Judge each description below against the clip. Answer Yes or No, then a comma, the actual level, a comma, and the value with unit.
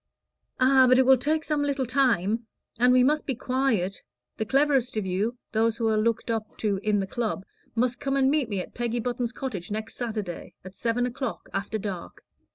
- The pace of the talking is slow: No, average, 200 wpm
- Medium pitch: No, high, 235 Hz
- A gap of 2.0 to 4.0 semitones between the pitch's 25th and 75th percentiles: Yes, average, 3.5 semitones